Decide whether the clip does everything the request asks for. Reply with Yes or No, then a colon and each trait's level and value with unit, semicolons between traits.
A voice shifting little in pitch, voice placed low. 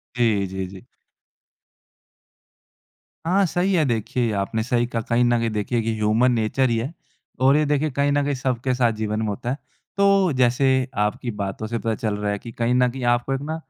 No: average, 3.6 semitones; low, 120 Hz